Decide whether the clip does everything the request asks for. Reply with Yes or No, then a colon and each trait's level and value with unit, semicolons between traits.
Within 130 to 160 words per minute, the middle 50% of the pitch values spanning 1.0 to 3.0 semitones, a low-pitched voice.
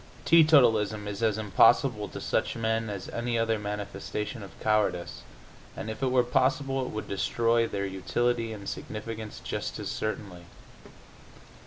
Yes: average, 145 wpm; narrow, 2.4 semitones; low, 110 Hz